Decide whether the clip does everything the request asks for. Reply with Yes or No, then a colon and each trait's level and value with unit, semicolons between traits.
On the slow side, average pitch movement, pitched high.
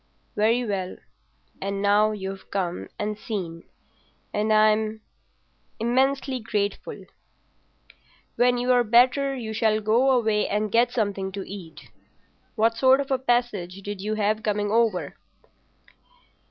Yes: slow, 120 wpm; average, 3.0 semitones; high, 215 Hz